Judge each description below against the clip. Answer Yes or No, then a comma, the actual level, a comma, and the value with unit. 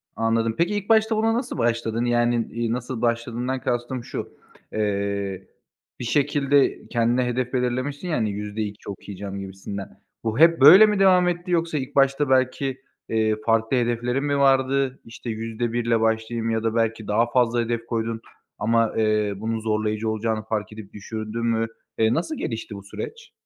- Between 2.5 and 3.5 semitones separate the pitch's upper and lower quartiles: Yes, average, 3.2 semitones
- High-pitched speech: No, low, 115 Hz